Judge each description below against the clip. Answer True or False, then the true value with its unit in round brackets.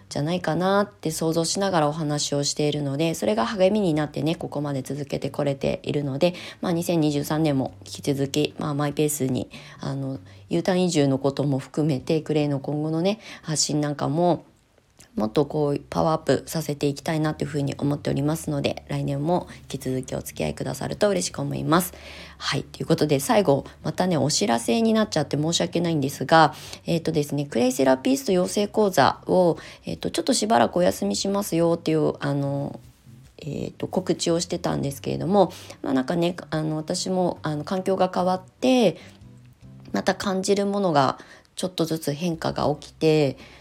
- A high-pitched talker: False (150 Hz)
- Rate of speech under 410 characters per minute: True (390 characters per minute)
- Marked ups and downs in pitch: False (3.6 semitones)